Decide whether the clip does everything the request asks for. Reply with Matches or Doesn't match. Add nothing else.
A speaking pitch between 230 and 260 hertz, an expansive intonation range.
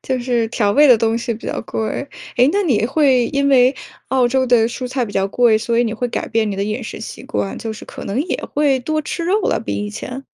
Doesn't match